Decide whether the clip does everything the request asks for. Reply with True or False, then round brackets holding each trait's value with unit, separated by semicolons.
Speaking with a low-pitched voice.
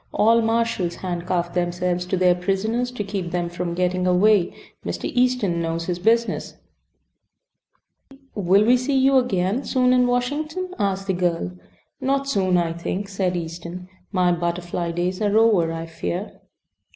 False (185 Hz)